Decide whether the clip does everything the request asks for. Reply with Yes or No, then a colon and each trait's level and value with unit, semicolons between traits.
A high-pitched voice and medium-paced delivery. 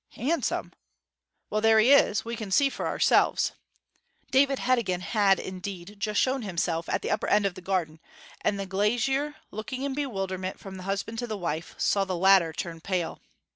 Yes: high, 200 Hz; average, 180 wpm